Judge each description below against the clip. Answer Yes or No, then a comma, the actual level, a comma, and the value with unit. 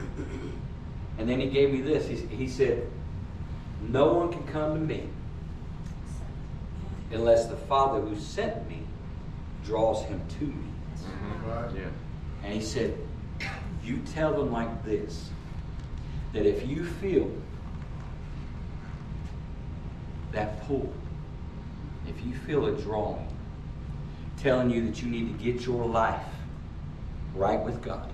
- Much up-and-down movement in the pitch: Yes, wide, 6.8 semitones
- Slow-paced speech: Yes, slow, 115 wpm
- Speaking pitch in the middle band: No, low, 105 Hz